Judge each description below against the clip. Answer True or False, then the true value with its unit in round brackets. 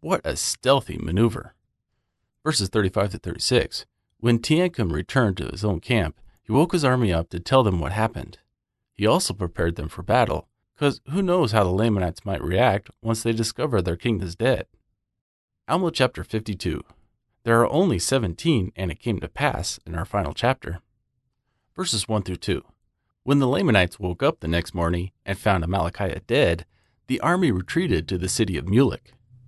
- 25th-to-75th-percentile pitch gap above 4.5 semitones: True (5.2 semitones)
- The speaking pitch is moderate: False (110 Hz)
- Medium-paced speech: True (175 wpm)